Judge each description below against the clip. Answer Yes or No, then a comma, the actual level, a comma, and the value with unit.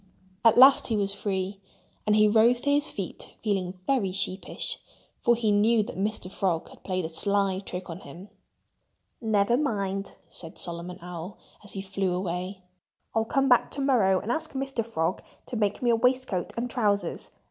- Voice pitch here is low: No, high, 200 Hz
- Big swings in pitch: No, average, 4.0 semitones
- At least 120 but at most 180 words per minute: Yes, average, 175 wpm